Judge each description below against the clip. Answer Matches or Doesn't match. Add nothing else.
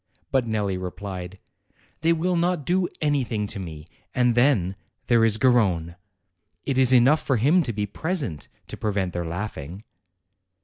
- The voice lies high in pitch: Doesn't match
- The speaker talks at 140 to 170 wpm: Matches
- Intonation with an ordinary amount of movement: Doesn't match